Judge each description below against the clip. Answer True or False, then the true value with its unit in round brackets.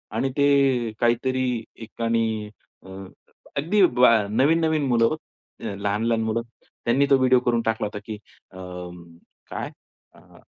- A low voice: True (120 Hz)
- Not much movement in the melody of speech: False (3.5 semitones)